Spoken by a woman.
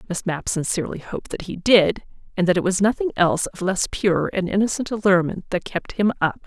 Yes: female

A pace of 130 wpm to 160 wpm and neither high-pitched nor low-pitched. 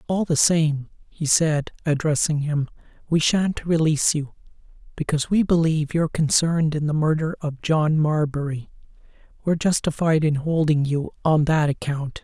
Yes: average, 145 wpm; medium, 155 Hz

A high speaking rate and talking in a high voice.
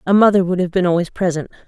No: fast, 250 wpm; medium, 180 Hz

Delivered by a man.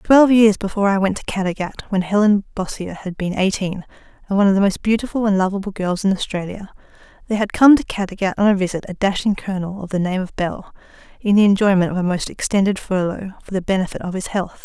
No: female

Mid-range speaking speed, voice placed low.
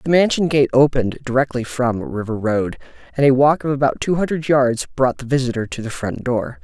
No: fast, 210 wpm; low, 130 Hz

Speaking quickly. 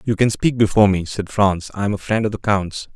Yes: fast, 285 wpm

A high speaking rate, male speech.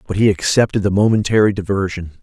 No: average, 160 wpm; male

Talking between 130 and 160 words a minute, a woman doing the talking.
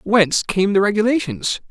No: average, 140 wpm; male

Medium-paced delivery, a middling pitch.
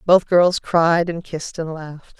Yes: average, 190 wpm; medium, 170 Hz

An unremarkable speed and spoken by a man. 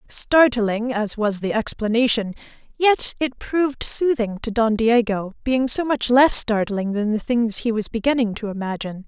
No: average, 165 wpm; female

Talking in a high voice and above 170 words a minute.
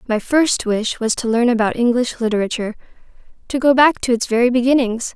Yes: high, 240 Hz; average, 185 wpm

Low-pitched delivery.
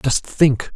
Yes: low, 130 Hz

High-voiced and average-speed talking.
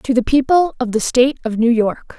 No: very high, 250 Hz; fast, 245 wpm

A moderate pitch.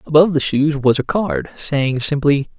Yes: medium, 145 Hz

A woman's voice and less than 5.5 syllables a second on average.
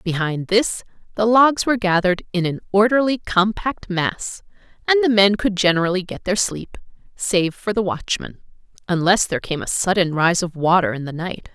Yes: female; 5.0 syllables/s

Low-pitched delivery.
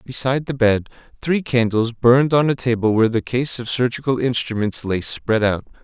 Yes: low, 120 Hz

